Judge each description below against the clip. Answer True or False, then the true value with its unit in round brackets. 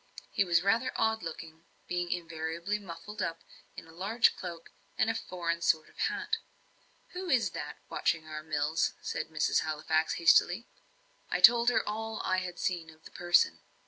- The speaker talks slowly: False (170 wpm)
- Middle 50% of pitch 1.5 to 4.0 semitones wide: False (4.9 semitones)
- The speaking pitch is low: False (175 Hz)